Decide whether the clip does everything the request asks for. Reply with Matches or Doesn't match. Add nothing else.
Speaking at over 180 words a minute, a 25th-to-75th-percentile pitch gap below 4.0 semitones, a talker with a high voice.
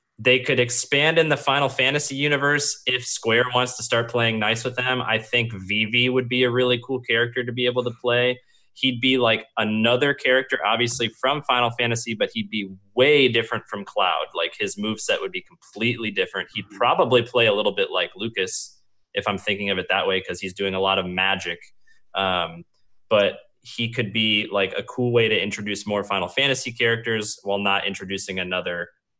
Doesn't match